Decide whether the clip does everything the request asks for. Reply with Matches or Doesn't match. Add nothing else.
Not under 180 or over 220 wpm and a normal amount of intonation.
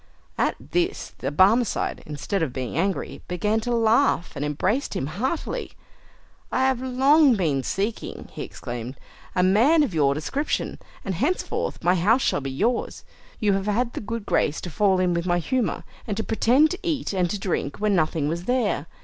Doesn't match